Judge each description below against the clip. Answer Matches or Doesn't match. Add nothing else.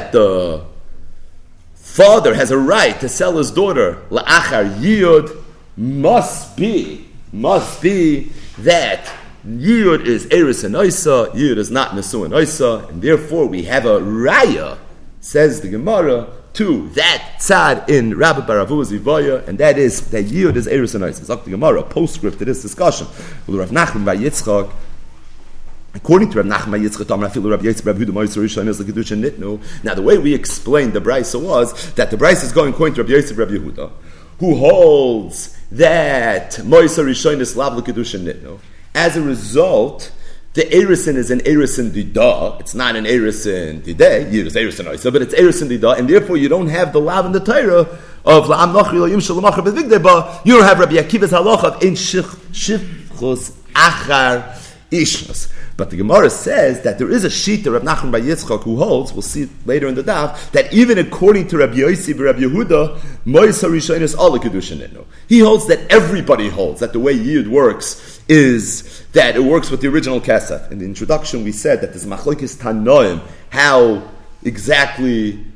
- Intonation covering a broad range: Matches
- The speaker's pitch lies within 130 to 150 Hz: Matches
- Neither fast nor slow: Matches